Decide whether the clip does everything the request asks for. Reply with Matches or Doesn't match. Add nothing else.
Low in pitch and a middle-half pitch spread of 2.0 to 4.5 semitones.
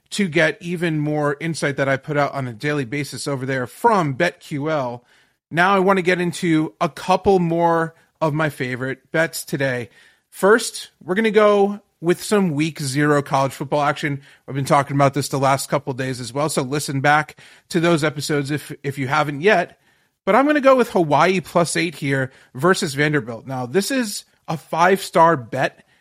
Doesn't match